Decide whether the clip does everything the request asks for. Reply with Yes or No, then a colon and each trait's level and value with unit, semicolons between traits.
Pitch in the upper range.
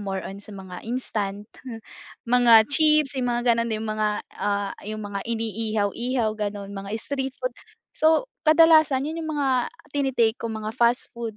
Yes: high, 230 Hz